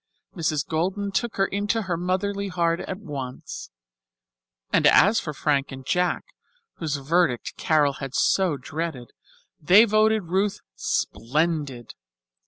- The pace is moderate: No, slow, 125 wpm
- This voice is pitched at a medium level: Yes, medium, 170 Hz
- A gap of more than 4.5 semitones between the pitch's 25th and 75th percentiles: Yes, wide, 5.4 semitones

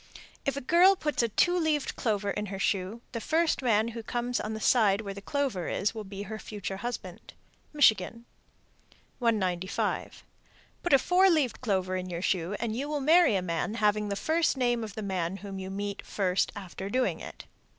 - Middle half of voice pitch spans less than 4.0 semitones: No, average, 4.7 semitones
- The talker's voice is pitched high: Yes, high, 215 Hz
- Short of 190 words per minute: No, average, 195 wpm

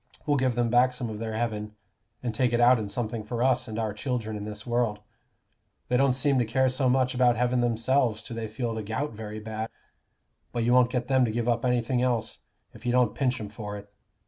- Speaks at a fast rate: Yes, fast, 235 wpm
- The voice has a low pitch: Yes, low, 120 Hz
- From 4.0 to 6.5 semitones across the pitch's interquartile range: No, narrow, 2.4 semitones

